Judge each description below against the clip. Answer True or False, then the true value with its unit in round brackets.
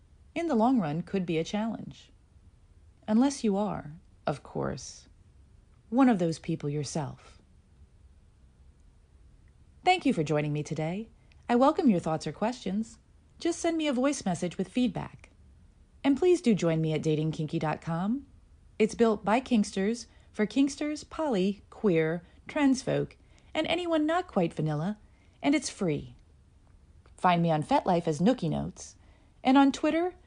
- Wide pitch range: True (9.0 semitones)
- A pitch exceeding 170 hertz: True (185 Hz)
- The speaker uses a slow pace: False (145 wpm)